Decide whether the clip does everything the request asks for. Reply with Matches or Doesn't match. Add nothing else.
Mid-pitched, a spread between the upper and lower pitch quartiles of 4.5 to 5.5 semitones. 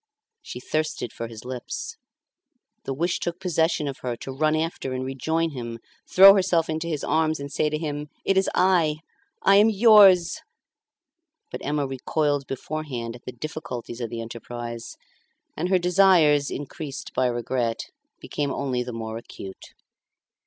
Matches